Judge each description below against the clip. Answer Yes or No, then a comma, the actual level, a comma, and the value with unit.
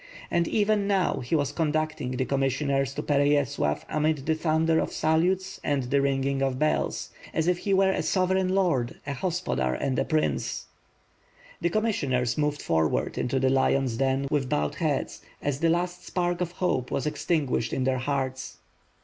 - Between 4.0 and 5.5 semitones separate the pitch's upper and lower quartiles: Yes, average, 4.6 semitones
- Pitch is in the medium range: Yes, medium, 145 Hz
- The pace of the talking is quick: No, average, 175 wpm